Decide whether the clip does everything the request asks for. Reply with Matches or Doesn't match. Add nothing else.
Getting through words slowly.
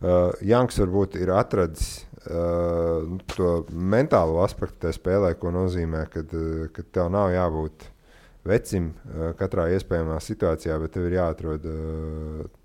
Matches